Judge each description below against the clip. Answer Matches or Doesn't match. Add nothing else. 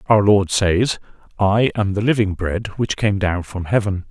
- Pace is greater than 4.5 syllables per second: Doesn't match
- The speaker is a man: Matches